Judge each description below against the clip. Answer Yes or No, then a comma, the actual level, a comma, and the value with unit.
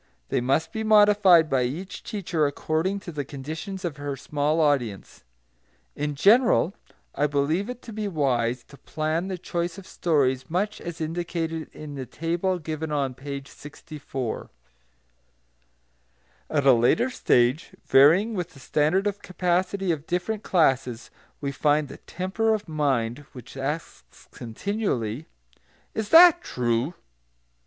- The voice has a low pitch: No, medium, 155 Hz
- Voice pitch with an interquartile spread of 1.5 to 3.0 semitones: No, average, 5.3 semitones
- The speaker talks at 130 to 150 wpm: Yes, average, 140 wpm